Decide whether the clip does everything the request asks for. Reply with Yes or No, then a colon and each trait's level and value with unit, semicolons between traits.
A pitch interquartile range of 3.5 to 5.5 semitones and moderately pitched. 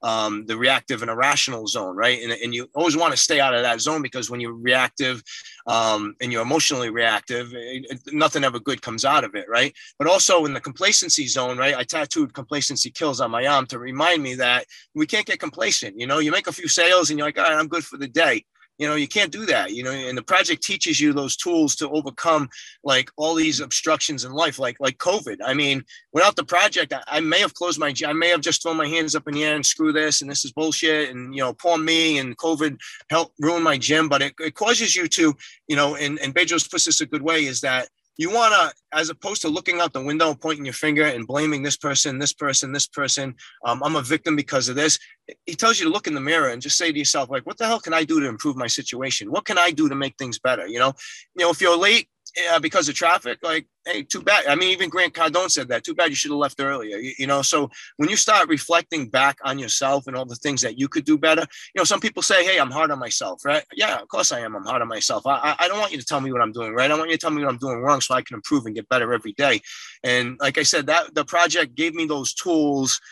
Yes: average, 3.8 semitones; medium, 150 Hz